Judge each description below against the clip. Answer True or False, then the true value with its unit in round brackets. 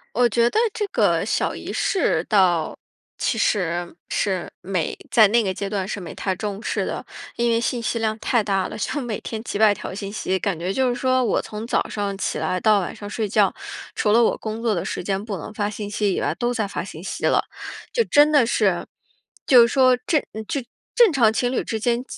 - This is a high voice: True (215 Hz)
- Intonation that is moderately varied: True (3.5 semitones)